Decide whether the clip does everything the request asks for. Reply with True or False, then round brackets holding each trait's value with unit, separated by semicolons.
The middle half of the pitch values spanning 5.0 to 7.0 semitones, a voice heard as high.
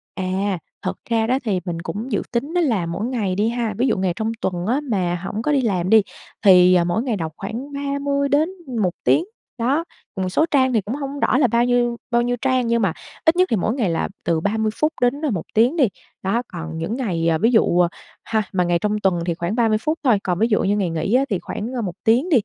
True (5.4 semitones; 220 Hz)